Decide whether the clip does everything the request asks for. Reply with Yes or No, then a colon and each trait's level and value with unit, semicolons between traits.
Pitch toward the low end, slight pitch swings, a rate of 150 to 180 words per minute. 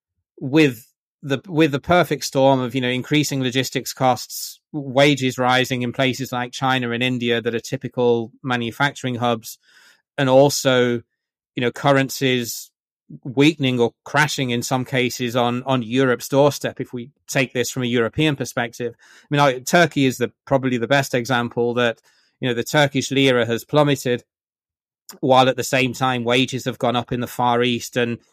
Yes: low, 130 Hz; narrow, 2.1 semitones; average, 165 wpm